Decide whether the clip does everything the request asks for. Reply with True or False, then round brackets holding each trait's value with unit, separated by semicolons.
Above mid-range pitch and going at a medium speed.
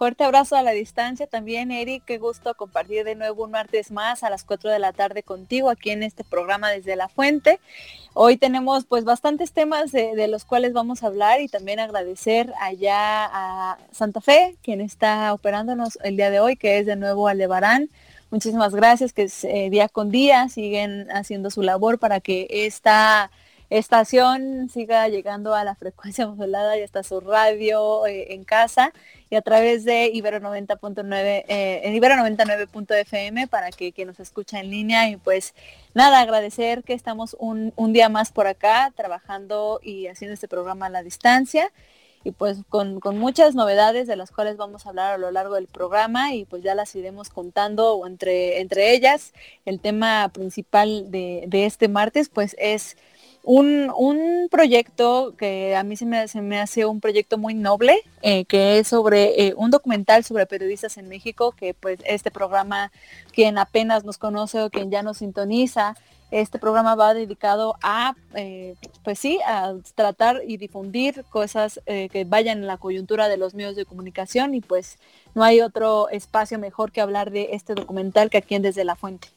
True (215 Hz; 185 wpm)